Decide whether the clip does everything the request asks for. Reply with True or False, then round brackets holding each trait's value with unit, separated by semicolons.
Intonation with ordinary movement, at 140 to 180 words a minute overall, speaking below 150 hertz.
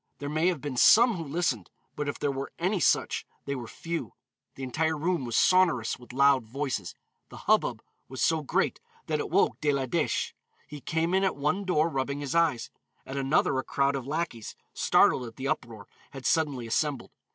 False (3.7 semitones; 195 wpm; 140 Hz)